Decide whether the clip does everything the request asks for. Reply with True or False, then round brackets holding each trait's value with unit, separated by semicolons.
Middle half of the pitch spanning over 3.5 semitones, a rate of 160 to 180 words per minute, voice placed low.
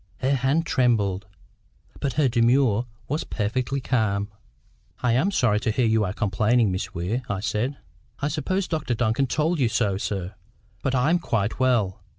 True (4.5 semitones; 165 wpm; 120 Hz)